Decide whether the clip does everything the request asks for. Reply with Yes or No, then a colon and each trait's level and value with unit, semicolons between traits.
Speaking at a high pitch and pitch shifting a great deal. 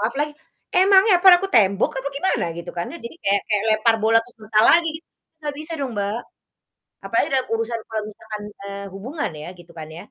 Yes: high, 225 Hz; wide, 6.6 semitones